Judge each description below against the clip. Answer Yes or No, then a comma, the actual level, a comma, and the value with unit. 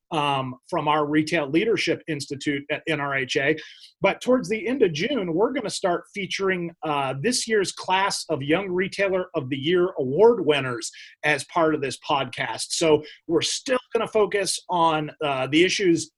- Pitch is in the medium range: Yes, medium, 170 Hz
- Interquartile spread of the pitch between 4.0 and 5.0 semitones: Yes, average, 4.7 semitones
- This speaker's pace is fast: No, average, 170 wpm